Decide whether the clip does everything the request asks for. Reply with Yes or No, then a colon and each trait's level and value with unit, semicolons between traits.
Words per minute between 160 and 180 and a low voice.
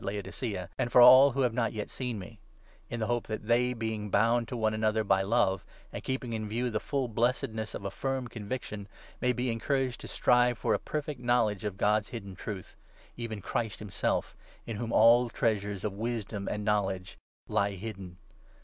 No: fast, 205 wpm; low, 110 Hz